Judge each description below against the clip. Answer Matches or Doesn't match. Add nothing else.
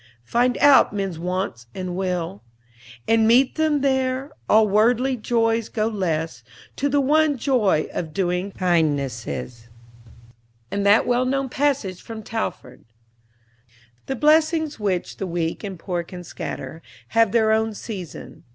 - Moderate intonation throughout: Doesn't match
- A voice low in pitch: Doesn't match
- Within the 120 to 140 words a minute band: Matches